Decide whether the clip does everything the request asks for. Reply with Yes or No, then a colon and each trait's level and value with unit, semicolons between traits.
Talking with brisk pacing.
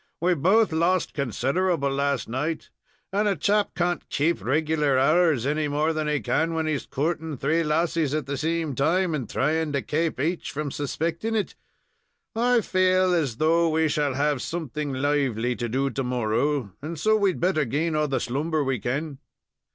No: average, 175 wpm